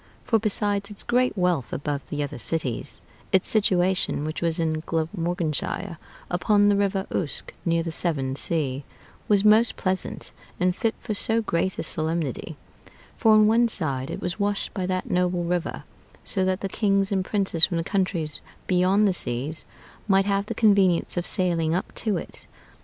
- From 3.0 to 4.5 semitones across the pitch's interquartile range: Yes, average, 3.6 semitones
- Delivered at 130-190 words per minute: Yes, average, 170 wpm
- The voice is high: No, medium, 180 Hz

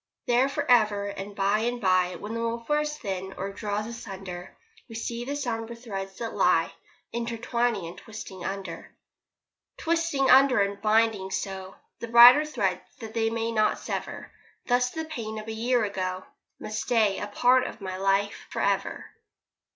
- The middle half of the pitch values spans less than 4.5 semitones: Yes, average, 3.6 semitones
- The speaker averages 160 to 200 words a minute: Yes, average, 165 wpm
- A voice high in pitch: Yes, high, 225 Hz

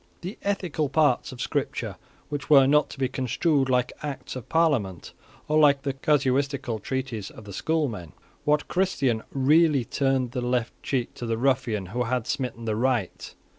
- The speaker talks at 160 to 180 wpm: Yes, average, 165 wpm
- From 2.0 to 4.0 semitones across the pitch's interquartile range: Yes, average, 3.5 semitones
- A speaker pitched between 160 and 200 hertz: No, low, 130 Hz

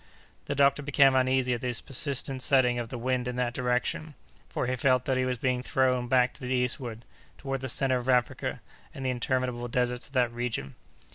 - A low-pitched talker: Yes, low, 125 Hz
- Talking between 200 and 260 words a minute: Yes, fast, 205 wpm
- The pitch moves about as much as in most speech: No, narrow, 1.3 semitones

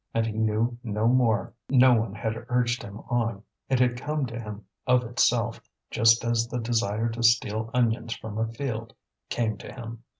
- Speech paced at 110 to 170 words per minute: No, average, 180 wpm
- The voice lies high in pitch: No, low, 115 Hz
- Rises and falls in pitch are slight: Yes, narrow, 1.6 semitones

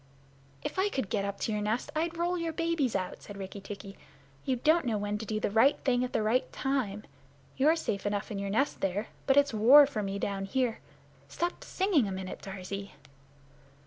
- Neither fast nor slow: No, fast, 210 wpm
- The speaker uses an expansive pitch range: Yes, wide, 6.1 semitones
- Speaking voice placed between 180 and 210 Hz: No, high, 220 Hz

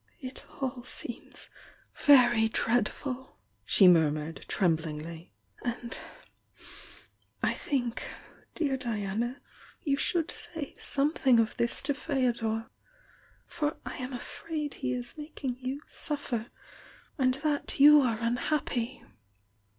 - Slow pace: Yes, slow, 110 wpm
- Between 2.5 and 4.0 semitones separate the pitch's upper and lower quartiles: No, average, 4.4 semitones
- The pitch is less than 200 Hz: No, very high, 250 Hz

